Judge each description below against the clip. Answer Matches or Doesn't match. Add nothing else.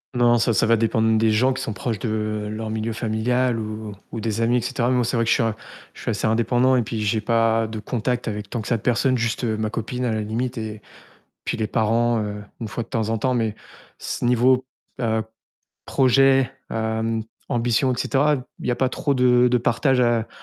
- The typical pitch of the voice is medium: Doesn't match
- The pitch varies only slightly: Matches